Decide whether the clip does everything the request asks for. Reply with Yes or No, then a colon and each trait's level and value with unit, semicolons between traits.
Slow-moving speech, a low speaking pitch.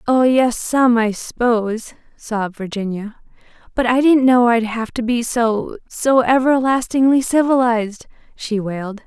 No: slow, 120 wpm; high, 235 Hz